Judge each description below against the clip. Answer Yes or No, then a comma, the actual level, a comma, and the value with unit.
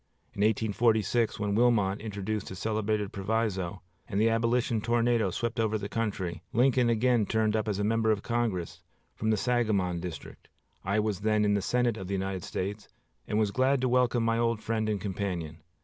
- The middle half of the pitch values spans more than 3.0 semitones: No, average, 2.7 semitones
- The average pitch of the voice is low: Yes, low, 110 Hz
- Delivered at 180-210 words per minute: Yes, average, 185 wpm